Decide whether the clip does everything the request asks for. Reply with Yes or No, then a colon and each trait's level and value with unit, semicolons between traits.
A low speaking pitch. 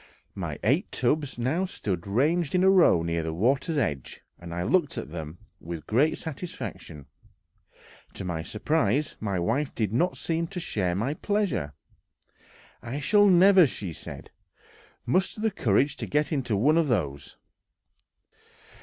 Yes: low, 130 Hz